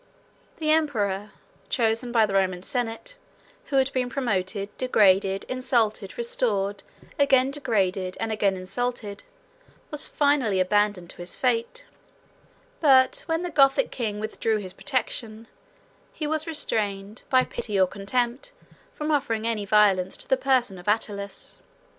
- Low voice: No, high, 225 Hz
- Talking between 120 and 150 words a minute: Yes, slow, 135 wpm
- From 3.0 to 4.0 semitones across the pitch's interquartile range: No, average, 4.8 semitones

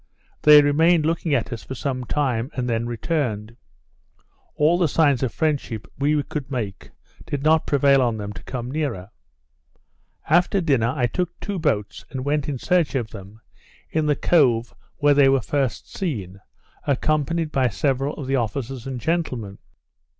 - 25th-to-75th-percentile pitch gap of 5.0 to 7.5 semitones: No, average, 4.4 semitones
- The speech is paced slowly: No, average, 165 wpm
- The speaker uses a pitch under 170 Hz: Yes, low, 135 Hz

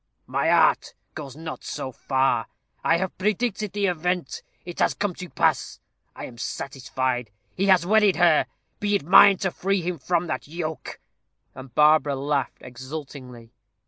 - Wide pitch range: Yes, wide, 5.7 semitones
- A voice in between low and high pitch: Yes, medium, 160 Hz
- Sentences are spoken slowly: No, average, 155 wpm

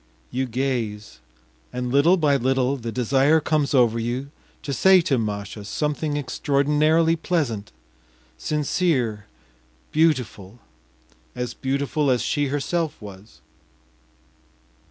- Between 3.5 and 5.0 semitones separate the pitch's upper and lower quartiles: Yes, average, 4.3 semitones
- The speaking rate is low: Yes, slow, 105 wpm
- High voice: No, low, 135 Hz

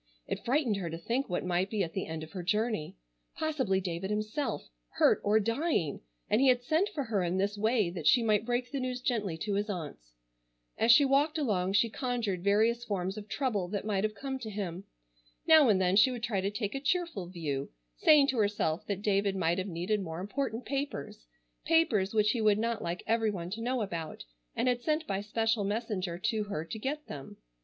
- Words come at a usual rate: No, fast, 215 wpm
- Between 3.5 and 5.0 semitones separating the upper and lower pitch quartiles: Yes, average, 4.6 semitones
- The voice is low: No, high, 210 Hz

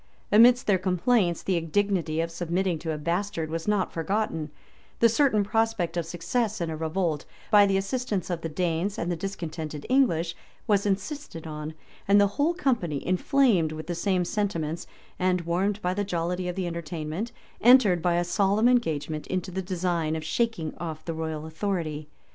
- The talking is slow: No, average, 175 wpm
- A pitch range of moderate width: Yes, average, 3.9 semitones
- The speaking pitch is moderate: Yes, medium, 180 Hz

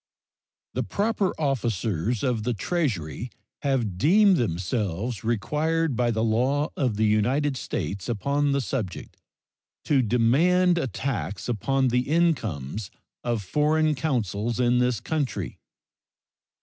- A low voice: Yes, low, 125 Hz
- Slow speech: Yes, slow, 120 wpm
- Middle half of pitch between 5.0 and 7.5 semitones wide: Yes, wide, 5.4 semitones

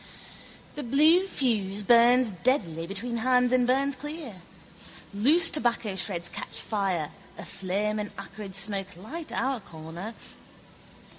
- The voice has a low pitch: No, high, 220 Hz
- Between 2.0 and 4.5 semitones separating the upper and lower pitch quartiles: No, average, 4.9 semitones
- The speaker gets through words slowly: Yes, slow, 120 wpm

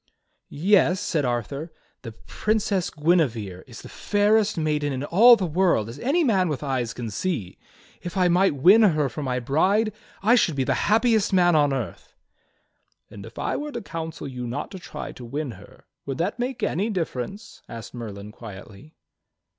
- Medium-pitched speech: Yes, medium, 155 Hz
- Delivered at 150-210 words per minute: Yes, average, 180 wpm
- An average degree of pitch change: No, wide, 7.8 semitones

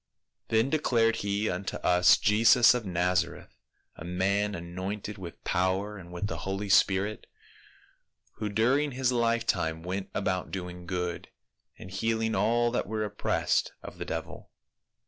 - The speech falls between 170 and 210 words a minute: No, average, 145 wpm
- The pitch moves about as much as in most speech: Yes, average, 3.7 semitones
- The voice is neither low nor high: No, low, 100 Hz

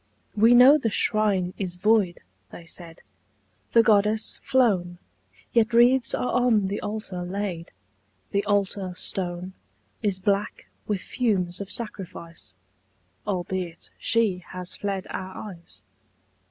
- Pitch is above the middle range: Yes, high, 200 Hz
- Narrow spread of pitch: No, average, 3.3 semitones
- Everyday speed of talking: No, slow, 120 wpm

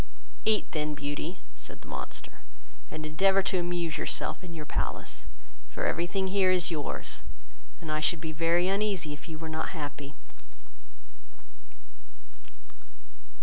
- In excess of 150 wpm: No, average, 140 wpm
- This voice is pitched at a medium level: Yes, medium, 165 Hz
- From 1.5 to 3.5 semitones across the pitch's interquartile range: Yes, average, 3.2 semitones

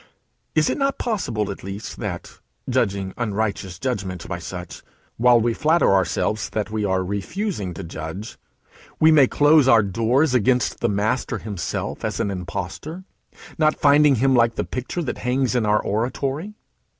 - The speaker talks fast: No, average, 160 wpm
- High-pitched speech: No, low, 115 Hz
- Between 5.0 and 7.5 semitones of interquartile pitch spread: Yes, wide, 5.5 semitones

